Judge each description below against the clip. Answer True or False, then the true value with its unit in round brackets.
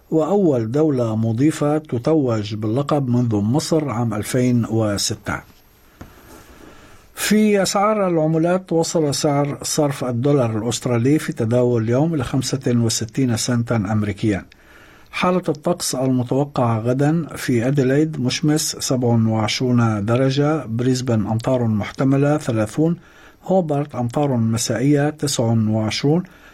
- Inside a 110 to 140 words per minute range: False (95 wpm)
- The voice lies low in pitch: True (130 Hz)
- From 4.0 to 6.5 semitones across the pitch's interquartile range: True (4.7 semitones)